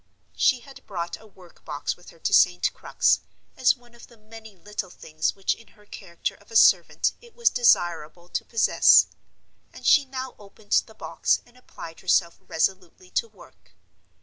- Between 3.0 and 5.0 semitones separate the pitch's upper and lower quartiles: No, wide, 5.5 semitones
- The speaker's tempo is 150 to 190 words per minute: Yes, average, 175 wpm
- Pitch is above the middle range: Yes, high, 210 Hz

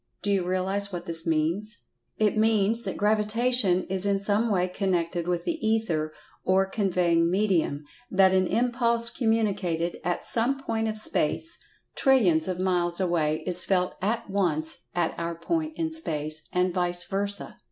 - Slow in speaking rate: No, average, 155 wpm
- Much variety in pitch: No, average, 3.9 semitones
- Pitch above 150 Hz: Yes, high, 190 Hz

